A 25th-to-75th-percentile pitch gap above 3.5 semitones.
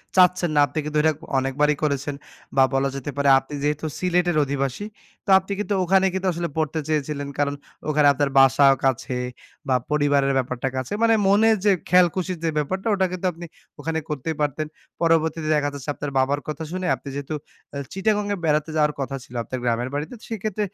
Yes: average, 4.3 semitones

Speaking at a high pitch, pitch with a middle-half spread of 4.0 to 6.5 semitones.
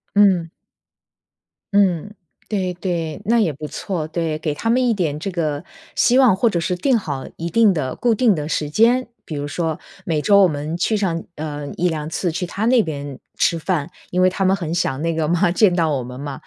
No: medium, 170 Hz; average, 4.6 semitones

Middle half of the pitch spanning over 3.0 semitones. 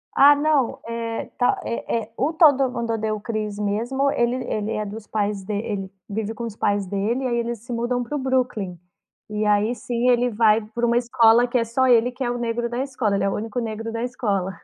No: narrow, 2.5 semitones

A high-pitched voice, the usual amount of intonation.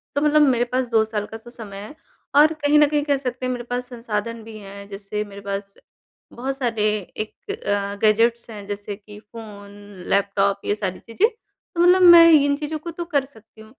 No: high, 230 Hz; wide, 5.7 semitones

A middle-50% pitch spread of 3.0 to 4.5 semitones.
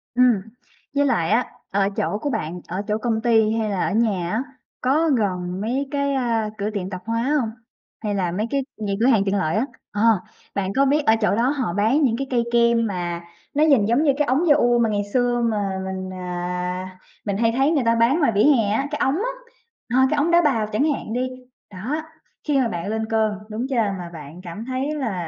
No: average, 5.0 semitones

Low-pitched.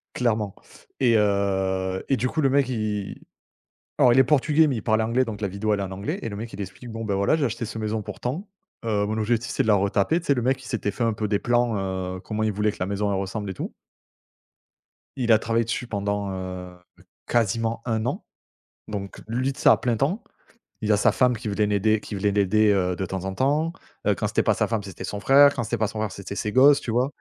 Yes: low, 110 Hz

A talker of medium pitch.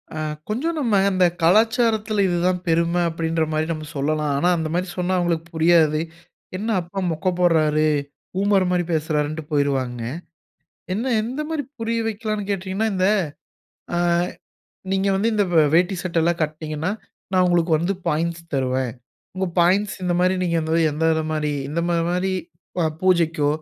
Yes: medium, 175 Hz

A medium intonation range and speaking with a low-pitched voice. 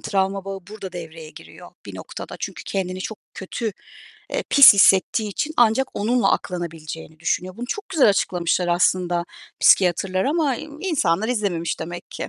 No: average, 4.5 semitones; high, 190 Hz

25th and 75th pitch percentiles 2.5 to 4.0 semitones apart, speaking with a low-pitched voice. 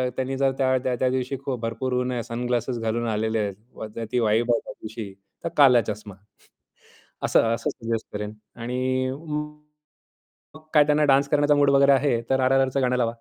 Yes: average, 2.8 semitones; low, 125 Hz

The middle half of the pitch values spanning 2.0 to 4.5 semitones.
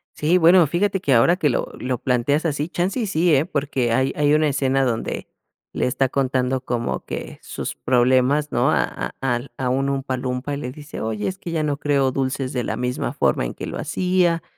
Yes: average, 3.5 semitones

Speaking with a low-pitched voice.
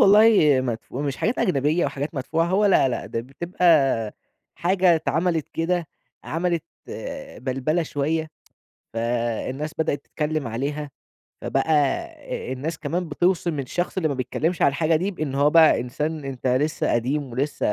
No: medium, 150 Hz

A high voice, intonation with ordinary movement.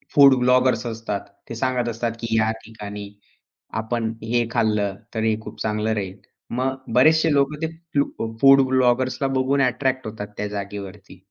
No: low, 115 Hz; average, 3.1 semitones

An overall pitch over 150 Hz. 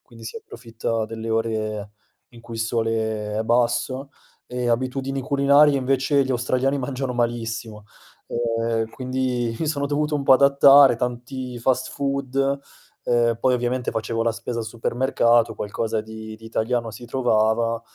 No: low, 120 Hz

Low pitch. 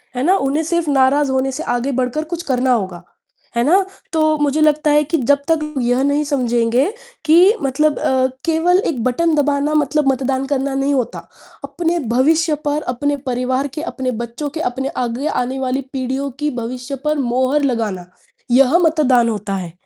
No: very high, 275 Hz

